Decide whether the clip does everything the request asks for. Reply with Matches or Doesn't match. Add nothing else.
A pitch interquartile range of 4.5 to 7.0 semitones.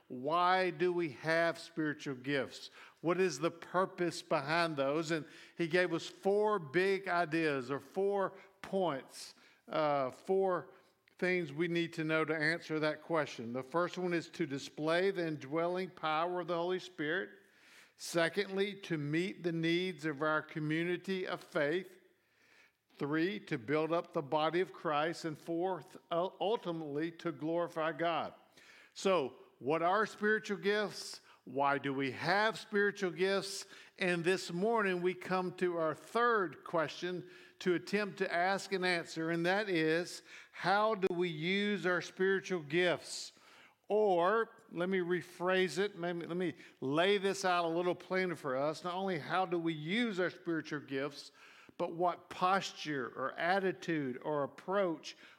Doesn't match